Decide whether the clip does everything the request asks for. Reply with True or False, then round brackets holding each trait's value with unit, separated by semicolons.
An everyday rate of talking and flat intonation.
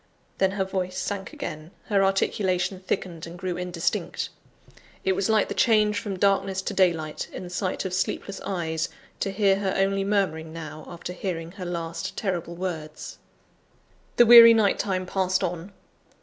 True (165 wpm; 2.3 semitones)